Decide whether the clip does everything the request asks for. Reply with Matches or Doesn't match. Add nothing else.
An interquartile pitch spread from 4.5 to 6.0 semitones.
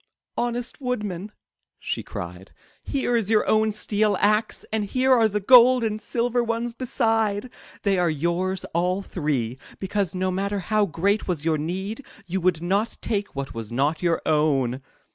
Matches